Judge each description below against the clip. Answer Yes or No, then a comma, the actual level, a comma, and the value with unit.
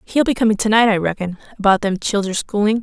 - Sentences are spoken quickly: Yes, fast, 235 wpm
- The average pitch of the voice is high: Yes, high, 210 Hz